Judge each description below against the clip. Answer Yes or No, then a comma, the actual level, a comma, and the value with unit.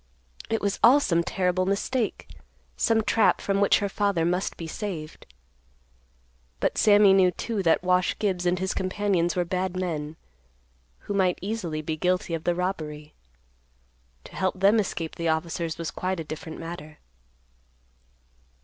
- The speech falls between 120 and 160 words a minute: Yes, average, 150 wpm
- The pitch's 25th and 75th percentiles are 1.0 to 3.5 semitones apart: Yes, average, 3.0 semitones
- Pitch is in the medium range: Yes, medium, 180 Hz